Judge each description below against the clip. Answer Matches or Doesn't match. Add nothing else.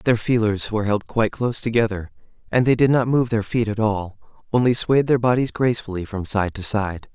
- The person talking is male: Matches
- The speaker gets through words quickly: Matches